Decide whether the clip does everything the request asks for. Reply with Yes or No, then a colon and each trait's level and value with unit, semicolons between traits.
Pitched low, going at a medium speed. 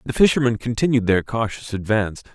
Yes: low, 115 Hz; average, 155 wpm